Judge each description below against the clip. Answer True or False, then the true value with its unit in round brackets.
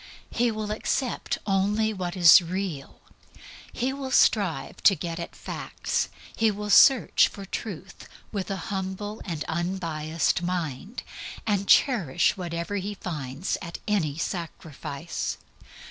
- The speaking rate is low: True (125 wpm)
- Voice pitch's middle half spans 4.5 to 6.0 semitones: False (3.7 semitones)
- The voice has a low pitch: False (190 Hz)